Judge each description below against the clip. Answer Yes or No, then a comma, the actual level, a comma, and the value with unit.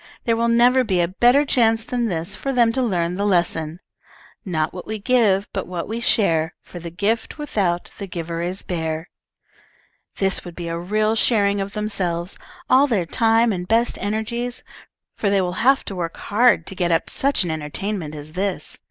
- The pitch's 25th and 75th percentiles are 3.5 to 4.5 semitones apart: No, average, 4.9 semitones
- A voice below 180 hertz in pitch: No, high, 200 Hz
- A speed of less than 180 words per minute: No, average, 190 wpm